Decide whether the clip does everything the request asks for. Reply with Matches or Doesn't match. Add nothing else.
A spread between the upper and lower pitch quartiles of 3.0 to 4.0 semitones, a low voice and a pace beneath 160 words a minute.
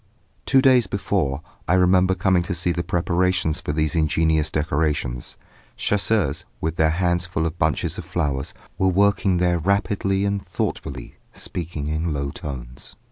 Matches